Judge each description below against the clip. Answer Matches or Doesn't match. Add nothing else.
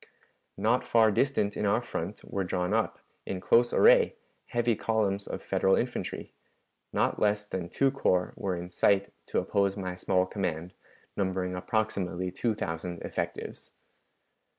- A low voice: Matches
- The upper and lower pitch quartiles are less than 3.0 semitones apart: Doesn't match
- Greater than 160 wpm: Doesn't match